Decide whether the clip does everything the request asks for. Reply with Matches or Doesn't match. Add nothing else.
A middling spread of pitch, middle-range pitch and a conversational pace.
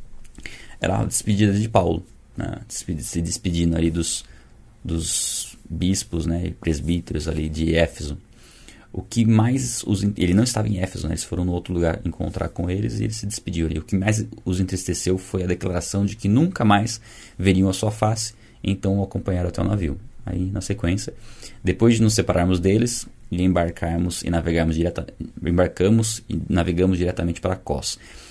Doesn't match